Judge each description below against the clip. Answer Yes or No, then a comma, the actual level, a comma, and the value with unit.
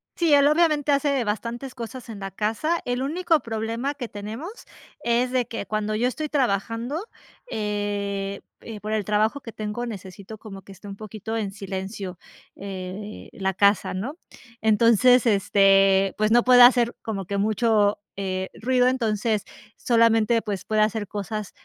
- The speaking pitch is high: Yes, high, 220 Hz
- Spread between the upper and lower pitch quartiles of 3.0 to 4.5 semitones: Yes, average, 3.5 semitones